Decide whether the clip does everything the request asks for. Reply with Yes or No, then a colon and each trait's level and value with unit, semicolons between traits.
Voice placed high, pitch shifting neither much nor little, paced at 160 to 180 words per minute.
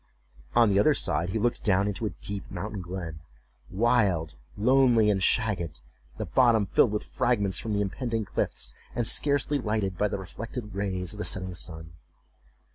No: low, 105 Hz; average, 3.6 semitones; average, 170 wpm